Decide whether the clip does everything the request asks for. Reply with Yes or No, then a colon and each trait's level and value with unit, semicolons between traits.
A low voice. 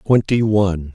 Yes: low, 100 Hz